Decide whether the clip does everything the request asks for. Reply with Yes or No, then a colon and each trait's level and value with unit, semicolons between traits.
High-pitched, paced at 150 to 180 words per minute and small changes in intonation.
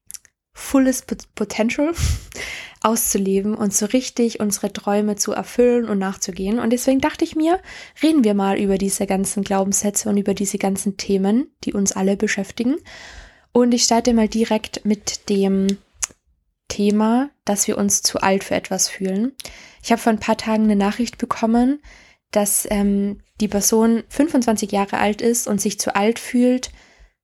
No: high, 215 Hz; average, 155 wpm; average, 3.2 semitones